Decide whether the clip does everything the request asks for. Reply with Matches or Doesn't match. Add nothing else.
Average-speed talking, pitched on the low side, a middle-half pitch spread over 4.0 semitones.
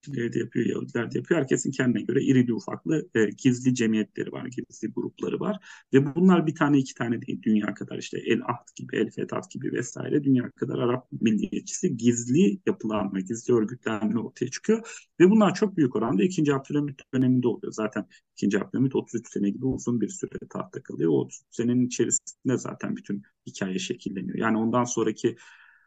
Matches